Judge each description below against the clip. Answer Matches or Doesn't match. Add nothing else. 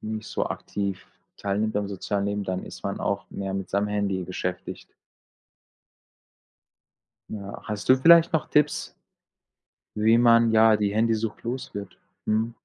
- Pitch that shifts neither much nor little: Doesn't match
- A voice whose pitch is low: Matches